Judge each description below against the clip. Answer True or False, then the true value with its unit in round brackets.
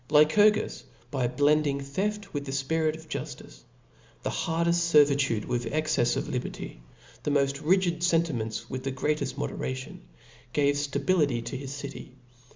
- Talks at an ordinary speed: True (145 wpm)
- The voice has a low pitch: False (145 Hz)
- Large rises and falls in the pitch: False (3.3 semitones)